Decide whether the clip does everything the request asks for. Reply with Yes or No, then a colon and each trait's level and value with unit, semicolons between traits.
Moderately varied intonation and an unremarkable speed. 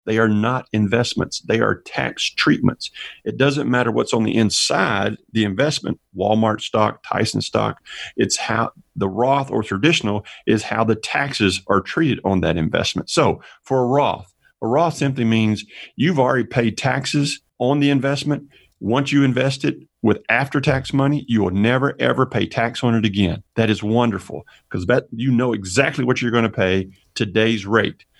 Yes: average, 4.2 semitones; average, 175 wpm